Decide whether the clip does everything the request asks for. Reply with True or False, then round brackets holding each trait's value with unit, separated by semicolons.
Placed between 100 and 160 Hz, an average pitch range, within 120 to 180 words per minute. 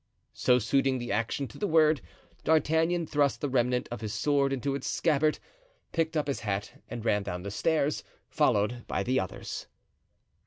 True (135 Hz; 4.9 semitones; 170 wpm)